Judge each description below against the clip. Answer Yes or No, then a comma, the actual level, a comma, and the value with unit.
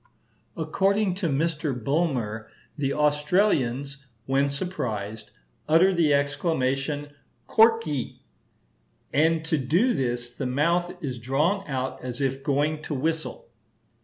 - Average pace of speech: No, slow, 110 wpm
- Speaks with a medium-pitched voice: Yes, medium, 145 Hz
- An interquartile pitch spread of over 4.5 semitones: No, average, 3.9 semitones